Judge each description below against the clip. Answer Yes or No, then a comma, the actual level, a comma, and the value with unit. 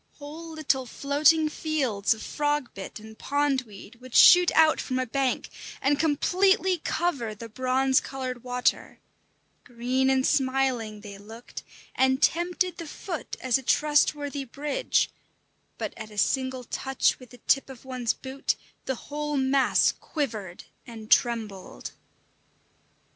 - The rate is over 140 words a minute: No, slow, 135 wpm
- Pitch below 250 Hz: No, very high, 265 Hz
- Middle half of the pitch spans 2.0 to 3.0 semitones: No, average, 3.7 semitones